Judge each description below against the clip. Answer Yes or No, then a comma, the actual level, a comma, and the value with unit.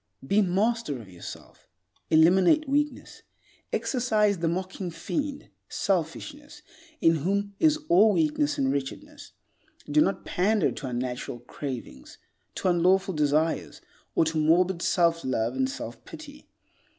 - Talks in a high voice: No, medium, 175 Hz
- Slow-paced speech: Yes, slow, 125 wpm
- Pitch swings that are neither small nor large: No, wide, 5.9 semitones